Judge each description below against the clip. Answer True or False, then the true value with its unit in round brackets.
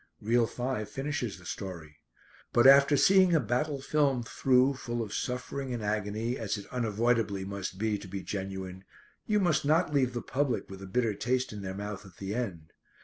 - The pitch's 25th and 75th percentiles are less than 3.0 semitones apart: False (4.9 semitones)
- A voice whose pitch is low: True (115 Hz)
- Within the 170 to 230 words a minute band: True (190 wpm)